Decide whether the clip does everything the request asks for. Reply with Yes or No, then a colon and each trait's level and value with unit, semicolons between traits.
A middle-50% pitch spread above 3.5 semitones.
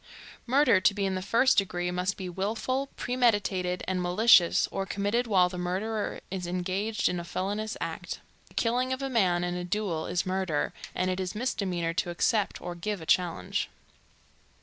No: average, 3.2 semitones